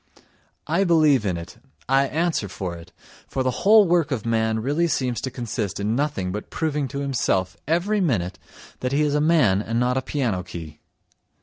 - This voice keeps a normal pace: Yes, average, 190 wpm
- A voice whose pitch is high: No, low, 130 Hz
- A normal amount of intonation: No, wide, 6.5 semitones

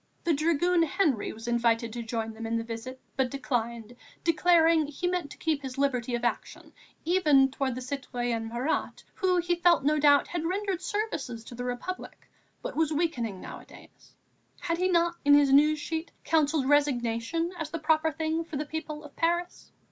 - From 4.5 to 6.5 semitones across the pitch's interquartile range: Yes, average, 5.3 semitones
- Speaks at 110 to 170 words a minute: No, average, 180 wpm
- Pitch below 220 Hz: No, very high, 290 Hz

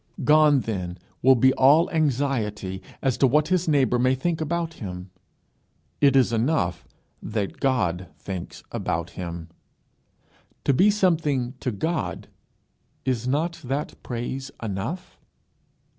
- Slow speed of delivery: Yes, slow, 125 wpm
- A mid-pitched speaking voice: No, low, 130 Hz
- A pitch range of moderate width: No, wide, 6.1 semitones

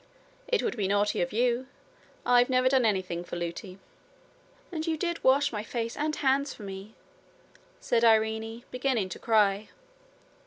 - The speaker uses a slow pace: No, average, 155 wpm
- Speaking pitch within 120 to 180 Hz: No, high, 230 Hz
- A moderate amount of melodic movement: Yes, average, 4.3 semitones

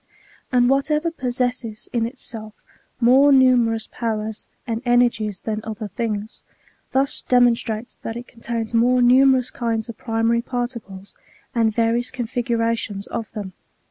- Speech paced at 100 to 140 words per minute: Yes, slow, 135 wpm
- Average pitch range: No, narrow, 2.0 semitones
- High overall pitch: Yes, high, 235 Hz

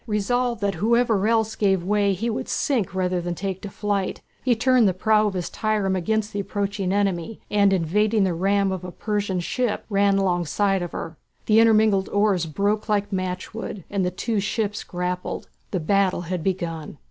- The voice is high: Yes, high, 200 Hz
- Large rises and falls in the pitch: No, narrow, 2.5 semitones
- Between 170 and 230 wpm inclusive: Yes, average, 180 wpm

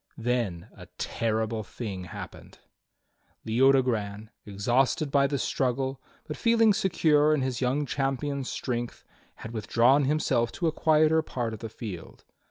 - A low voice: Yes, low, 130 Hz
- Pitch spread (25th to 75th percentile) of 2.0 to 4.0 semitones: No, average, 4.4 semitones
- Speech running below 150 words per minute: Yes, slow, 135 wpm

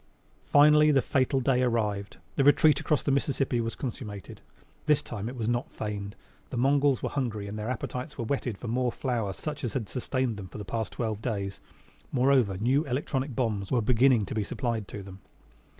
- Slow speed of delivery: No, average, 190 wpm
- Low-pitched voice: Yes, low, 120 Hz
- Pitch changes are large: No, average, 4.1 semitones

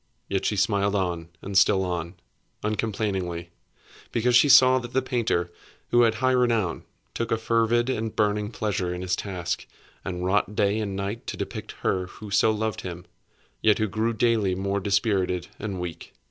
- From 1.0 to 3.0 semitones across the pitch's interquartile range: No, average, 3.4 semitones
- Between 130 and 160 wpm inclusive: No, average, 175 wpm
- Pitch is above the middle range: No, low, 105 Hz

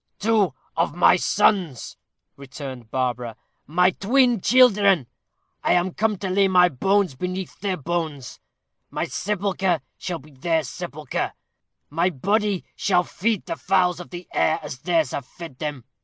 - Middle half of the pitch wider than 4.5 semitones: Yes, average, 4.9 semitones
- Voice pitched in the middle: Yes, medium, 180 Hz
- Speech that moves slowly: No, average, 145 wpm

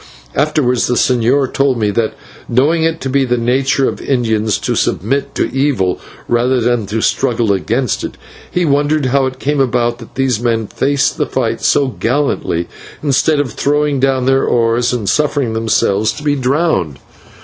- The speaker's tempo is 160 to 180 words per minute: Yes, average, 170 wpm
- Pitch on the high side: No, low, 130 Hz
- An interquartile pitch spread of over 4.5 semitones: No, average, 3.3 semitones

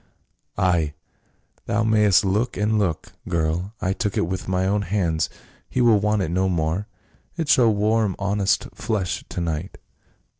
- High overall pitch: No, low, 100 Hz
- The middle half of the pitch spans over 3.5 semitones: No, average, 3.0 semitones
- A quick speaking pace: No, average, 155 wpm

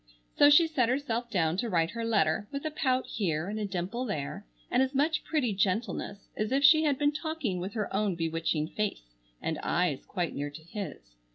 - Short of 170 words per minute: No, fast, 205 wpm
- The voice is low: No, high, 215 Hz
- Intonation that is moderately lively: No, wide, 7.4 semitones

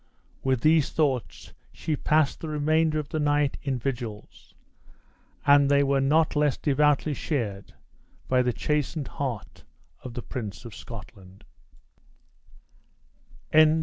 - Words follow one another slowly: Yes, slow, 120 wpm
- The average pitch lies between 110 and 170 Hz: Yes, medium, 140 Hz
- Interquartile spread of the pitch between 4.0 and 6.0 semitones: No, average, 3.6 semitones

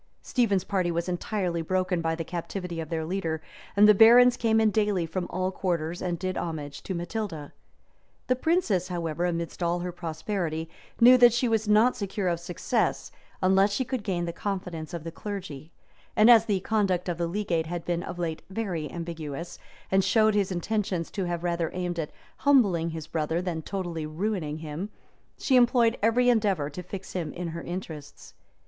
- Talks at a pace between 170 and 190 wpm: Yes, average, 185 wpm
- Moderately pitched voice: Yes, medium, 180 Hz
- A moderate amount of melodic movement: Yes, average, 3.8 semitones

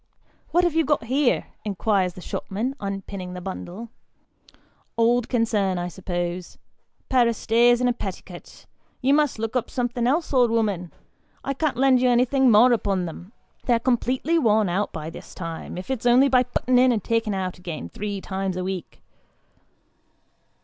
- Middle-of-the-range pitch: No, high, 225 Hz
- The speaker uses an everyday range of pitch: Yes, average, 4.9 semitones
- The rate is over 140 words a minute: Yes, average, 175 wpm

